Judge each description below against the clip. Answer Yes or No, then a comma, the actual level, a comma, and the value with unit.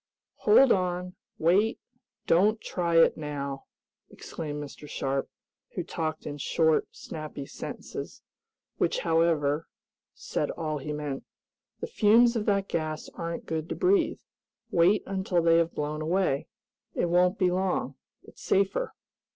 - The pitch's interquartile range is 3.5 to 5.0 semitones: Yes, average, 3.9 semitones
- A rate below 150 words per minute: Yes, slow, 135 wpm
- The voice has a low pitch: No, medium, 165 Hz